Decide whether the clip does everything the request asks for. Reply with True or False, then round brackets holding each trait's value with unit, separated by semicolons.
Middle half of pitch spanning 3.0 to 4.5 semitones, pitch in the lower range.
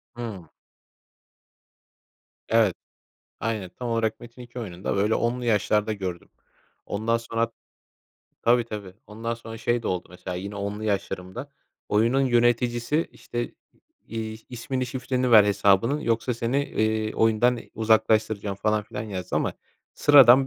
False (2.5 semitones; 115 Hz)